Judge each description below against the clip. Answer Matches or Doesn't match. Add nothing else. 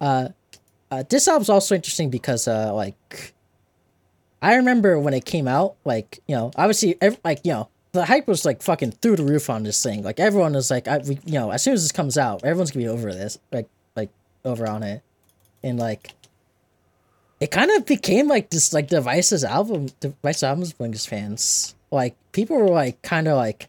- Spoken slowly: Doesn't match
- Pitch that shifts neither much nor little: Doesn't match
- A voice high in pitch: Doesn't match